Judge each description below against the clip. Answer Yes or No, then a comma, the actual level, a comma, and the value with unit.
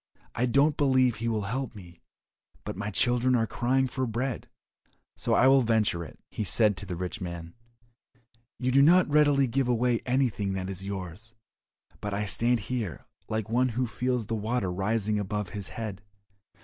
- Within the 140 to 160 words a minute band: No, average, 175 wpm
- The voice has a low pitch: Yes, low, 115 Hz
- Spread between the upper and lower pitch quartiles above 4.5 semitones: No, average, 3.9 semitones